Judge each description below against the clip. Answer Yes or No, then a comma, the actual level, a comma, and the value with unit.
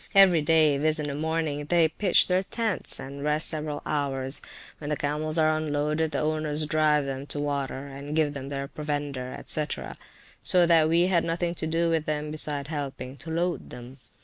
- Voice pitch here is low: No, medium, 150 Hz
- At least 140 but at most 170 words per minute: No, average, 190 wpm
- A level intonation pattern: Yes, narrow, 2.0 semitones